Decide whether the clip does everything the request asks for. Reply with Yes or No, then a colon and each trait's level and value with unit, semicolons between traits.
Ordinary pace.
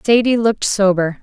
Yes: average, 145 wpm